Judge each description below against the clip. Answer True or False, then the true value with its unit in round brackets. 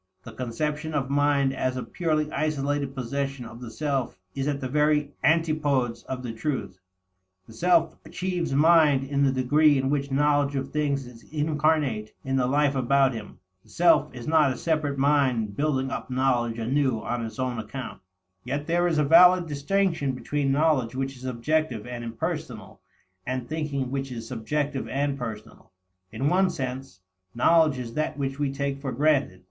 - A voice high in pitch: False (140 Hz)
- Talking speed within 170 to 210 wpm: True (175 wpm)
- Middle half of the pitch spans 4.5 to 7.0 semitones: False (2.9 semitones)